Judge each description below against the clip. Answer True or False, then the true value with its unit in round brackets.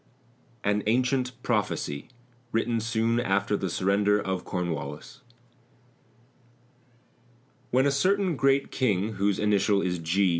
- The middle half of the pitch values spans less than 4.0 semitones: False (4.5 semitones)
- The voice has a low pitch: True (105 Hz)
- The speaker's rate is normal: False (110 wpm)